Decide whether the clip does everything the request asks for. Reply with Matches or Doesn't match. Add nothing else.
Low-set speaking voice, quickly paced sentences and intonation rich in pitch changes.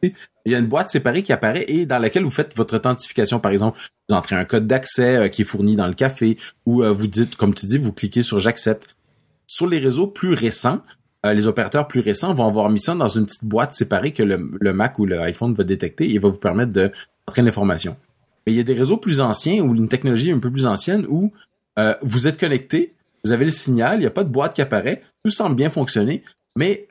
Doesn't match